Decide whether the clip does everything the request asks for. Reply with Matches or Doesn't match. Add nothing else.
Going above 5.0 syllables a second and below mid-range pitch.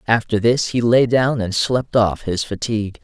Doesn't match